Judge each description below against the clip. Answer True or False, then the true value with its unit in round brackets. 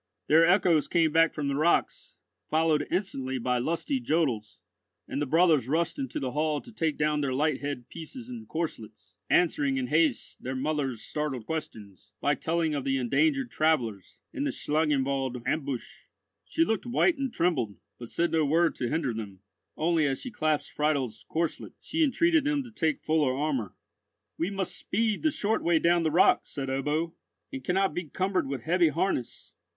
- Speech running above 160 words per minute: True (175 wpm)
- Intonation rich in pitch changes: False (4.4 semitones)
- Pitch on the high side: False (155 Hz)